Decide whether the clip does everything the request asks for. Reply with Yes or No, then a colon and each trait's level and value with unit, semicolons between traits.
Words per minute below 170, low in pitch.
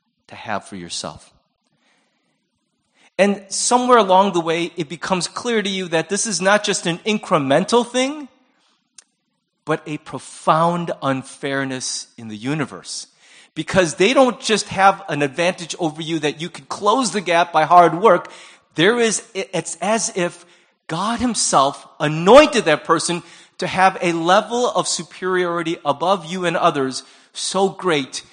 No: average, 145 wpm; medium, 175 Hz